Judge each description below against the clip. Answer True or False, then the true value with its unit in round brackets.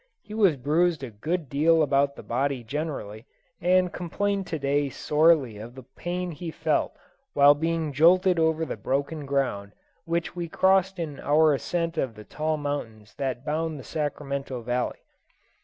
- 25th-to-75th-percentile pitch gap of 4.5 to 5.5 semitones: False (3.7 semitones)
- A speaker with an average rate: True (160 wpm)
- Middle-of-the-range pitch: True (150 Hz)